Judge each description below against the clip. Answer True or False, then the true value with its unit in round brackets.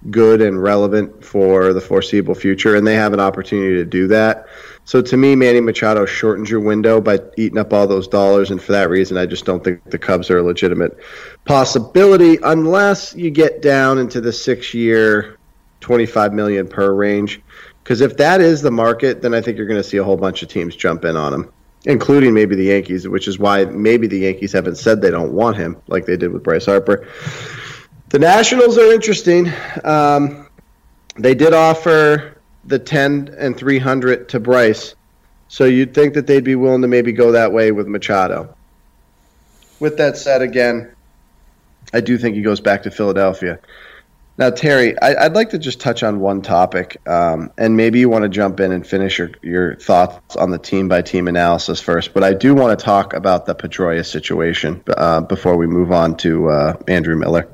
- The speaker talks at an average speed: True (195 wpm)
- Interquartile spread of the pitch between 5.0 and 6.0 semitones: True (5.4 semitones)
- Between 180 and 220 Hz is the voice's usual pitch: False (105 Hz)